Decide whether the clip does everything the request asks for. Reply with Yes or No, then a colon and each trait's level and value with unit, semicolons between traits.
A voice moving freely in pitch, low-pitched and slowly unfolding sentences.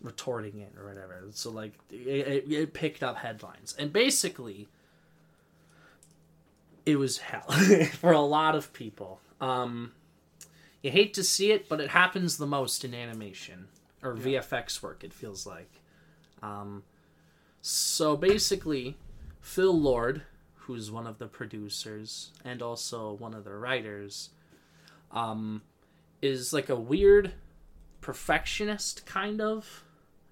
Yes: wide, 6.6 semitones; low, 130 Hz; slow, 130 wpm